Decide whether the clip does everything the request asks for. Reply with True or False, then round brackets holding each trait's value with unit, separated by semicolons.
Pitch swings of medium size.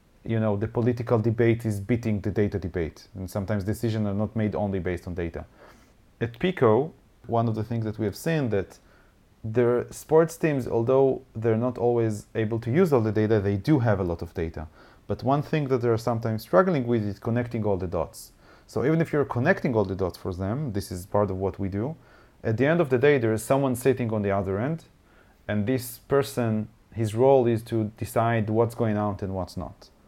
True (3.4 semitones)